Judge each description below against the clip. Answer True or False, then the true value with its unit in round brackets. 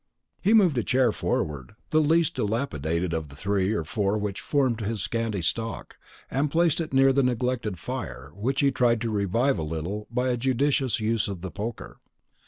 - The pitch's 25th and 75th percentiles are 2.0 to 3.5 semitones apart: False (5.2 semitones)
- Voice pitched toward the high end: False (115 Hz)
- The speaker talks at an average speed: True (190 wpm)